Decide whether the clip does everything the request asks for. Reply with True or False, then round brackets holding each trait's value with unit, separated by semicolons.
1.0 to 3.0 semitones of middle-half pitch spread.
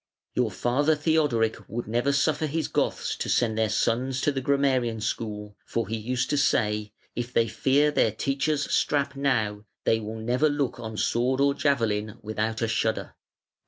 False (4.1 semitones)